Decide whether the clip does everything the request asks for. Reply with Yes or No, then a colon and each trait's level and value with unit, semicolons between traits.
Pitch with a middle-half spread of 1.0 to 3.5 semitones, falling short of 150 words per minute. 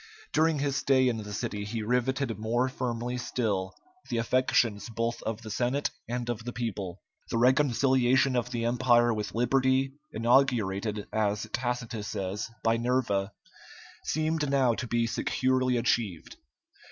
Yes: average, 2.7 semitones; average, 140 wpm